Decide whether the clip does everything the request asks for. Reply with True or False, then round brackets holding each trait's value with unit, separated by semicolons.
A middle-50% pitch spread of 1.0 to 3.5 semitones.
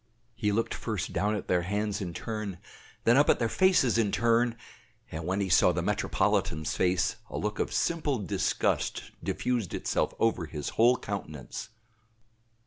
False (4.1 semitones)